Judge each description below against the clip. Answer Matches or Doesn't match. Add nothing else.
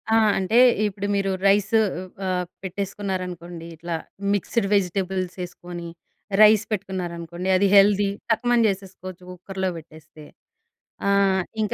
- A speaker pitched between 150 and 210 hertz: Matches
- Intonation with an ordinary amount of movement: Doesn't match